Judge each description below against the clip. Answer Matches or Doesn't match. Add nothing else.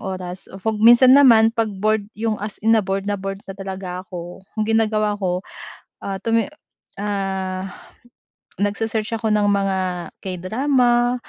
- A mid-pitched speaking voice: Doesn't match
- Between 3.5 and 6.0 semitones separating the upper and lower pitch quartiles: Doesn't match